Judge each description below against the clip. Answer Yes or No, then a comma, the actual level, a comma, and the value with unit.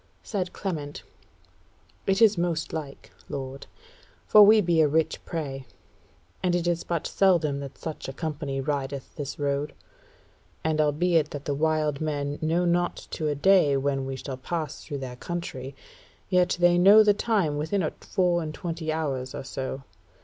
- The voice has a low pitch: No, medium, 155 Hz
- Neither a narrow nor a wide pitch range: Yes, average, 3.8 semitones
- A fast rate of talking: No, average, 165 wpm